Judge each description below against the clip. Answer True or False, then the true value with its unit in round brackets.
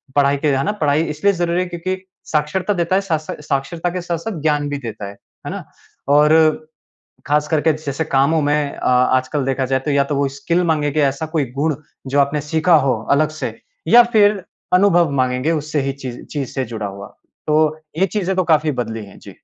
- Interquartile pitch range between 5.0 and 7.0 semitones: False (3.8 semitones)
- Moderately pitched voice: True (150 Hz)